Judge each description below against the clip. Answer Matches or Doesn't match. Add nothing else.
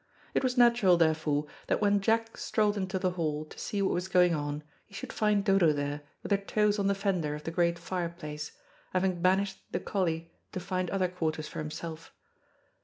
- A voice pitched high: Doesn't match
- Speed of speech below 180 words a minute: Doesn't match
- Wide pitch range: Doesn't match